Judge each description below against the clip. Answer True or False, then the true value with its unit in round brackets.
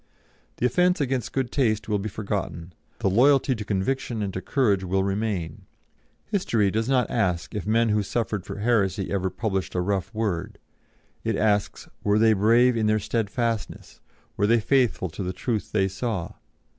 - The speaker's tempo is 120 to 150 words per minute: False (170 wpm)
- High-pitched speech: False (105 Hz)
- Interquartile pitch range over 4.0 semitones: False (3.4 semitones)